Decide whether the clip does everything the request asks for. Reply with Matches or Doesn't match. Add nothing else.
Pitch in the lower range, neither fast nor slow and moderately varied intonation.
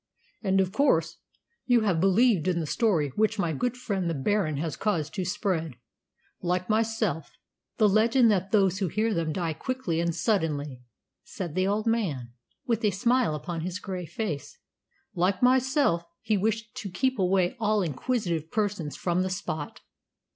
Doesn't match